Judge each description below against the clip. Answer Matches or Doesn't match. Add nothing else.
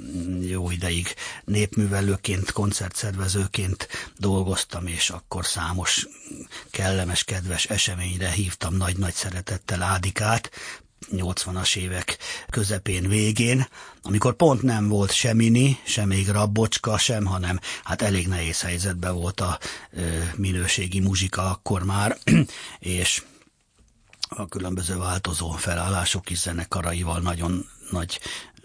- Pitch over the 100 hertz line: Doesn't match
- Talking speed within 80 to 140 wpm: Matches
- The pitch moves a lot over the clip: Doesn't match